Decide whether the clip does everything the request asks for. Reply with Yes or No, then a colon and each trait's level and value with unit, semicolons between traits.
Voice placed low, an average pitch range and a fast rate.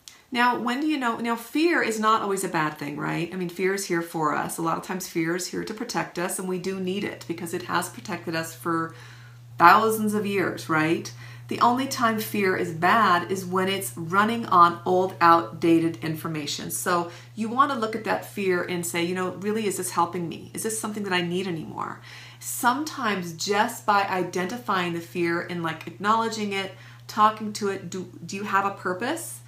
No: medium, 180 Hz; average, 3.9 semitones; fast, 210 wpm